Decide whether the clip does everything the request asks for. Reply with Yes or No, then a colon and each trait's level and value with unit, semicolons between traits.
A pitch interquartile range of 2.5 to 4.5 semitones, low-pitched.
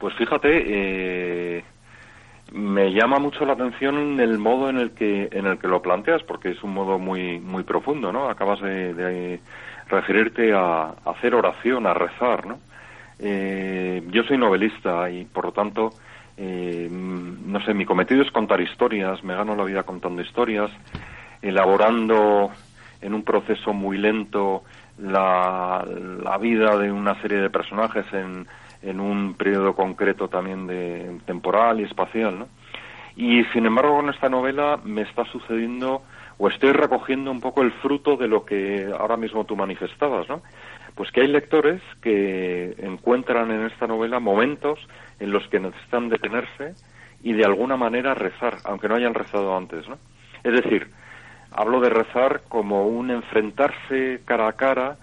Yes: average, 4.1 semitones; low, 105 Hz